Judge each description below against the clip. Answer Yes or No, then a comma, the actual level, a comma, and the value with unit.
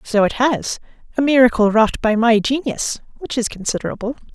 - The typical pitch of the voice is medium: No, high, 235 Hz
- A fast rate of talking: No, average, 150 wpm